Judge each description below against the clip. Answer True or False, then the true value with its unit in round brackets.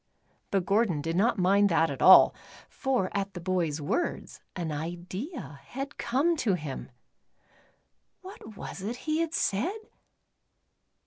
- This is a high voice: True (195 Hz)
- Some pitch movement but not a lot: False (6.7 semitones)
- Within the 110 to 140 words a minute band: True (135 wpm)